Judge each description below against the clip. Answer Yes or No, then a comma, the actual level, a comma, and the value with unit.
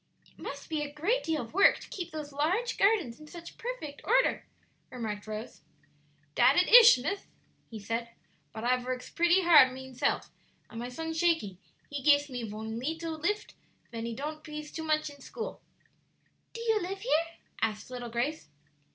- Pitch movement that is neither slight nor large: No, wide, 6.0 semitones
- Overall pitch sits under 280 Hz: No, very high, 300 Hz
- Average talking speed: Yes, average, 175 wpm